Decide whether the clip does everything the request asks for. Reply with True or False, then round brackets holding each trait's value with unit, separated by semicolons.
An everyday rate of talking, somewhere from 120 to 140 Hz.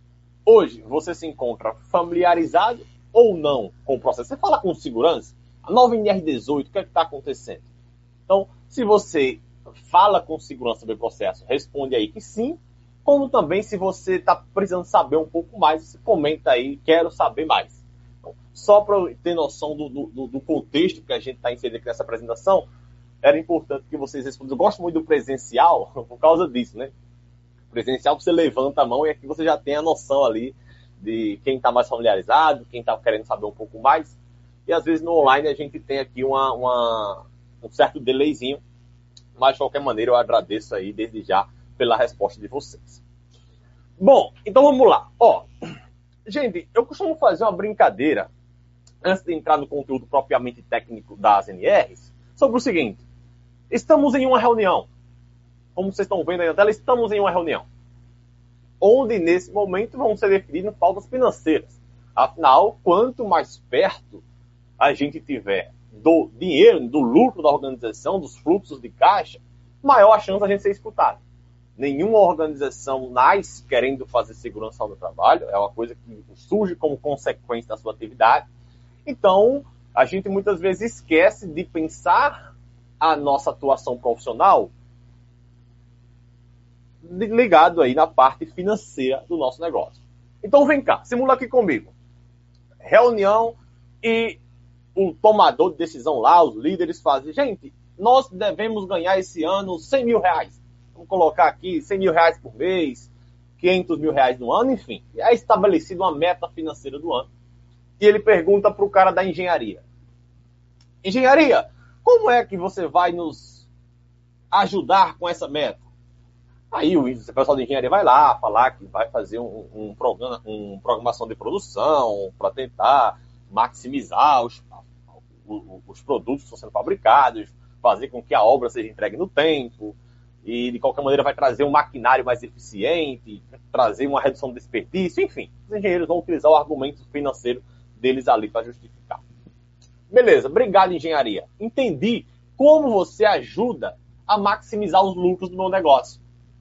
True (155 wpm; 135 Hz)